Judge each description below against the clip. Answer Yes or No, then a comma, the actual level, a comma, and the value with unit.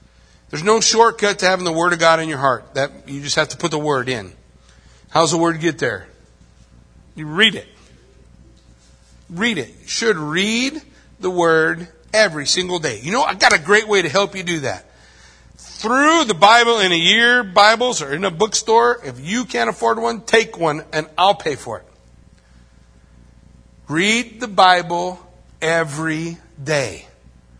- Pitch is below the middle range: No, medium, 165 Hz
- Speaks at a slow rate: No, average, 170 wpm